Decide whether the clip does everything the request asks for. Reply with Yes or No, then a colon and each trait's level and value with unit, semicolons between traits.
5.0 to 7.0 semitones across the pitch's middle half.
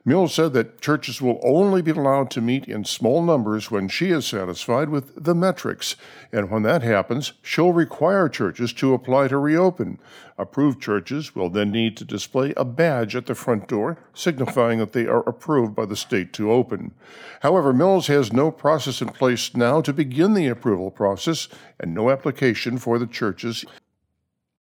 Yes: average, 5.3 semitones